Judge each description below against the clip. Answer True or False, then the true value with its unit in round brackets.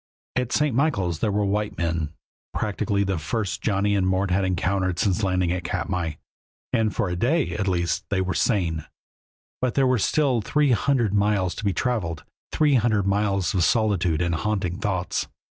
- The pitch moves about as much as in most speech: True (3.5 semitones)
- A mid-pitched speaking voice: False (100 Hz)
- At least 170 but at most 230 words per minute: True (175 wpm)